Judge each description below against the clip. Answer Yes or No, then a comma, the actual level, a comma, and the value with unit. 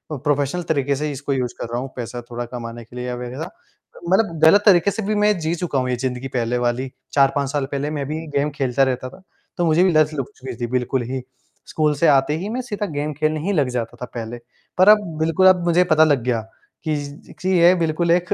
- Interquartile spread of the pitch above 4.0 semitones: Yes, average, 5.0 semitones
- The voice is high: No, medium, 145 Hz